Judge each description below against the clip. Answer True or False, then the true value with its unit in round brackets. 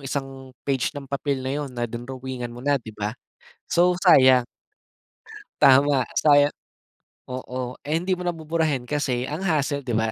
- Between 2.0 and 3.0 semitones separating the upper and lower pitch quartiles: True (2.7 semitones)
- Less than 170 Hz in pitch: True (135 Hz)